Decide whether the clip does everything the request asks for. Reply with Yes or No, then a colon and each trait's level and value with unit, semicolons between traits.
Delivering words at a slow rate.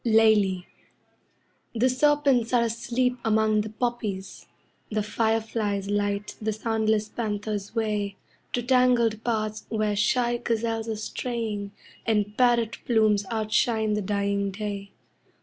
Yes: slow, 115 wpm